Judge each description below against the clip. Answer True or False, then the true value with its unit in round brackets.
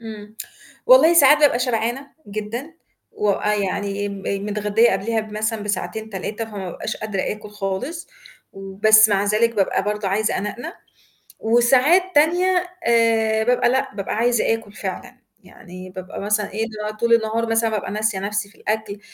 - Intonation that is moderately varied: False (2.3 semitones)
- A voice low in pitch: False (215 Hz)